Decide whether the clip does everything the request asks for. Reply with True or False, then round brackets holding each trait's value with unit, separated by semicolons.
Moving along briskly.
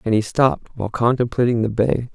False (195 wpm)